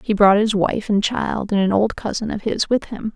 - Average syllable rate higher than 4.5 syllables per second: Yes, 4.9 syllables/s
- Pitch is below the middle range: No, high, 210 Hz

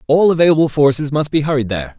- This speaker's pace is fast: Yes, fast, 210 wpm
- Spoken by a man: Yes, male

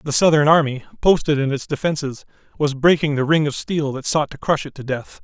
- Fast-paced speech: Yes, fast, 230 wpm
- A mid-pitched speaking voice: Yes, medium, 145 Hz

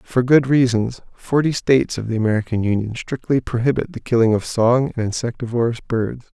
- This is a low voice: Yes, low, 120 Hz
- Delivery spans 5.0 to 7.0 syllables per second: Yes, 5.6 syllables/s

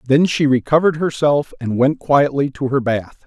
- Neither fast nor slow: Yes, average, 185 wpm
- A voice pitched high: No, medium, 140 Hz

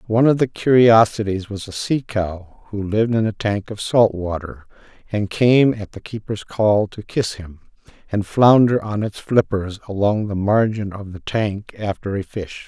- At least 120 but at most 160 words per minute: No, average, 185 wpm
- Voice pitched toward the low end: Yes, low, 105 Hz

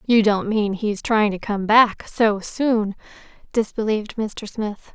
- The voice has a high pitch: Yes, high, 215 Hz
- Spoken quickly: No, average, 160 wpm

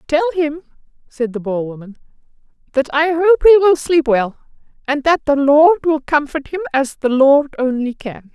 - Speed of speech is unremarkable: Yes, average, 180 wpm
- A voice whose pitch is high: Yes, very high, 290 Hz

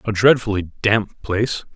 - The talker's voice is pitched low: Yes, low, 105 Hz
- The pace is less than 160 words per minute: Yes, slow, 135 wpm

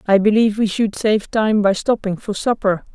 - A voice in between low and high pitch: No, high, 210 Hz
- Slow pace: No, fast, 205 wpm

